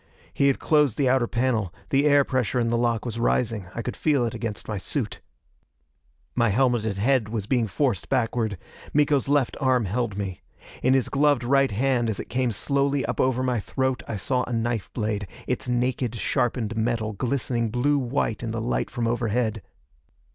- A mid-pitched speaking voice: No, low, 120 Hz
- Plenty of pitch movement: No, average, 2.9 semitones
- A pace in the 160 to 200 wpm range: Yes, average, 185 wpm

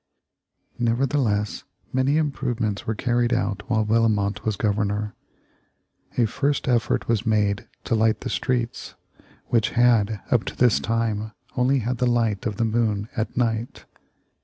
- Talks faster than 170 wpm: No, average, 140 wpm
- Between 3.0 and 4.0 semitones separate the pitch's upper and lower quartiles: No, narrow, 2.5 semitones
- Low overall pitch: Yes, low, 115 Hz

